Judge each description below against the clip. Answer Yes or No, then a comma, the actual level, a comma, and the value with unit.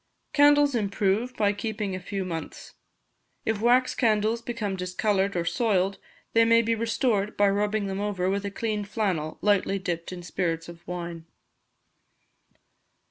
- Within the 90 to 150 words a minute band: Yes, average, 145 wpm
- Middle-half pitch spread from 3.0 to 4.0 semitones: Yes, average, 3.3 semitones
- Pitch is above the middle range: Yes, high, 205 Hz